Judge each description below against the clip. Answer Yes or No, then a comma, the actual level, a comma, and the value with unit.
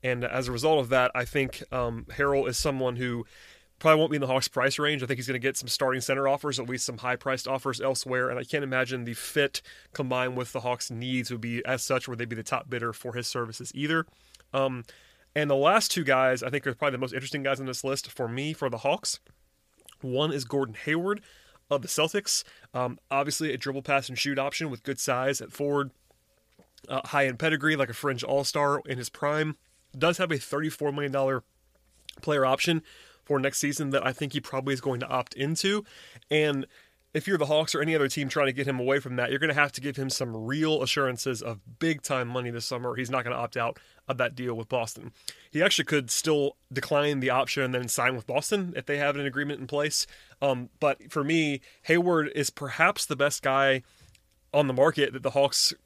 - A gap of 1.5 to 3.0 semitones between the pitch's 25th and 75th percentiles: Yes, narrow, 2.4 semitones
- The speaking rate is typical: No, fast, 230 wpm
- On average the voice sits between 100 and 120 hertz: No, low, 135 Hz